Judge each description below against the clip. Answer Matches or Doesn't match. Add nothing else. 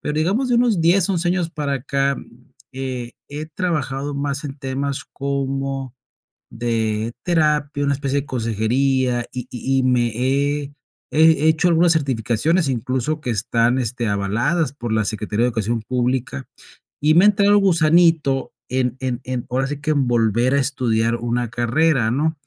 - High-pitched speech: Doesn't match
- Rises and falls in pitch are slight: Doesn't match